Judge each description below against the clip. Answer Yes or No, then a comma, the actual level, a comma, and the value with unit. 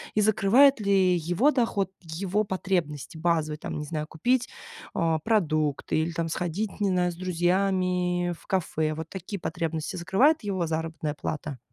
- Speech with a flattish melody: No, average, 3.6 semitones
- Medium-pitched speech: Yes, medium, 175 Hz